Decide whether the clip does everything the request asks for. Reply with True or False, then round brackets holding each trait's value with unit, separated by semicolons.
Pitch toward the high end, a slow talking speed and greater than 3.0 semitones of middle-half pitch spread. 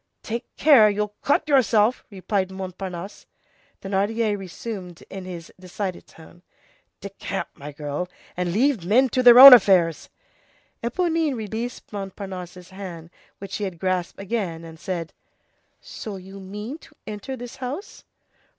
True (195 Hz; 130 wpm; 4.4 semitones)